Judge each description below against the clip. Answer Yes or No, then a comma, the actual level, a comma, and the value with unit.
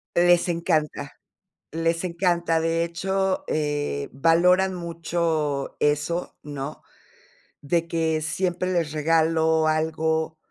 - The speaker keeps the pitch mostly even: Yes, narrow, 1.7 semitones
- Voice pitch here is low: No, medium, 165 Hz